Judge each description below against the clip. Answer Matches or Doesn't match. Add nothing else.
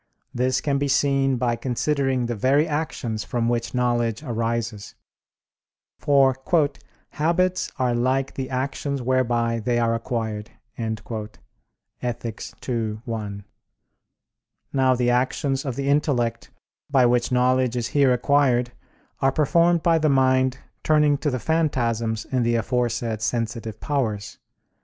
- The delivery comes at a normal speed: Doesn't match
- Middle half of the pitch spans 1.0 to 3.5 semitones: Matches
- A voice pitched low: Matches